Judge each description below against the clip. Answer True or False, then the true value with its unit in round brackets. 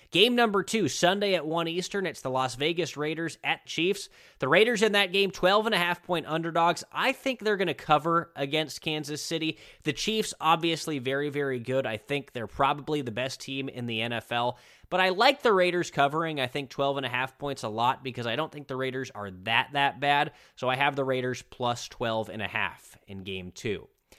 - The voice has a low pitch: False (145 Hz)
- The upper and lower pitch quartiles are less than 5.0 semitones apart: False (5.4 semitones)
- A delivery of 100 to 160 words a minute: False (195 wpm)